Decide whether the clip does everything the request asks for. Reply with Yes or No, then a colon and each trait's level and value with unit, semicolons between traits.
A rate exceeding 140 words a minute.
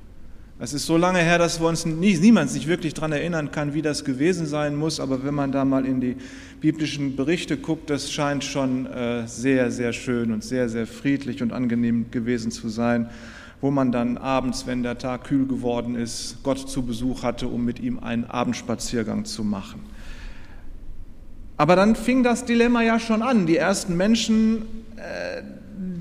Yes: average, 180 wpm